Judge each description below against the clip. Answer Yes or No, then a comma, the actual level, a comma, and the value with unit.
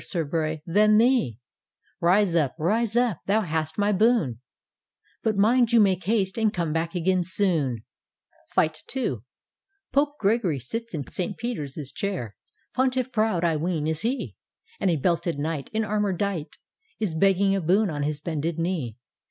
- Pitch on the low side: No, medium, 185 Hz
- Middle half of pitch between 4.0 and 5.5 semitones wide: Yes, average, 5.2 semitones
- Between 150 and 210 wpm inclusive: Yes, average, 160 wpm